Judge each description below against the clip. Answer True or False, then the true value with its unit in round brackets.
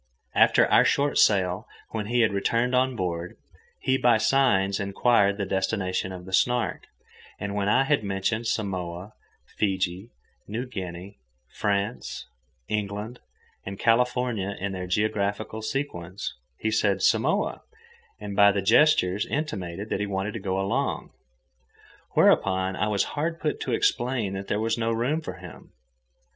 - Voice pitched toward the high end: False (105 Hz)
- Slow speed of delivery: False (145 wpm)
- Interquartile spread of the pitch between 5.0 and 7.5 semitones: False (3.4 semitones)